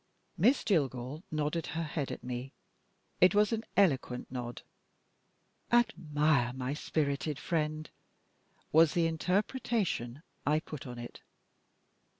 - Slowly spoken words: Yes, slow, 115 wpm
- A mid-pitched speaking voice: Yes, medium, 155 Hz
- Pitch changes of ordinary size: Yes, average, 4.7 semitones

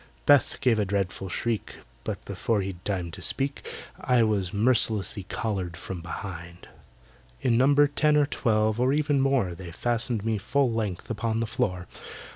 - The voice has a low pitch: Yes, low, 110 Hz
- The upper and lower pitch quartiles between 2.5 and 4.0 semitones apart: No, average, 4.9 semitones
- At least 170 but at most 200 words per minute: No, average, 160 wpm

